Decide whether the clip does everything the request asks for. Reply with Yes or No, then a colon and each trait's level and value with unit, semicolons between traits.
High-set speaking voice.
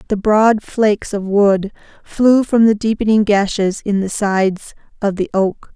Yes: high, 205 Hz